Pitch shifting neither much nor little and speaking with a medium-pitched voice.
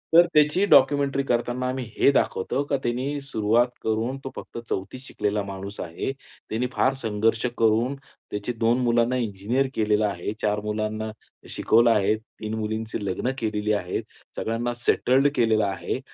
No: average, 3.3 semitones; low, 115 Hz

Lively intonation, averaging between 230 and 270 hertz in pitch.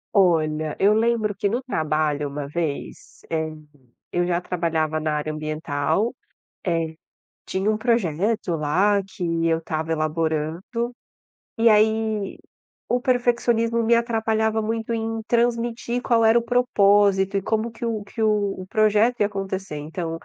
No: wide, 5.8 semitones; high, 200 Hz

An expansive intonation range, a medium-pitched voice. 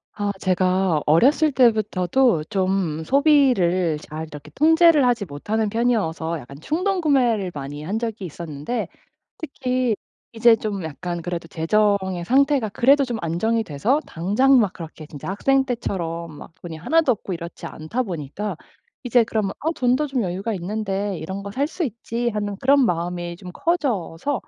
No: wide, 6.7 semitones; high, 205 Hz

